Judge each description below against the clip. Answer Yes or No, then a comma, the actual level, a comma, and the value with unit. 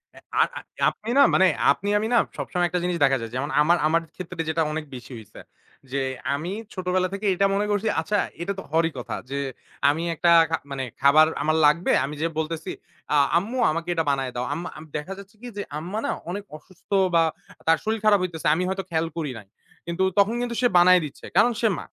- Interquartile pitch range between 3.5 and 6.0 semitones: Yes, average, 4.0 semitones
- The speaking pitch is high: No, medium, 170 Hz